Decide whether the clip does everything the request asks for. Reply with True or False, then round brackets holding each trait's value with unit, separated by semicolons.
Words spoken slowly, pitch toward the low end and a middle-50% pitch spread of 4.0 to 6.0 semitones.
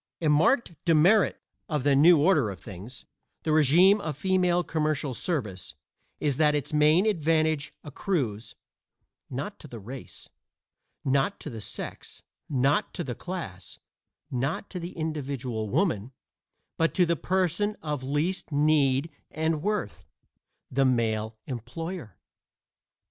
False (130 wpm; 150 Hz; 4.8 semitones)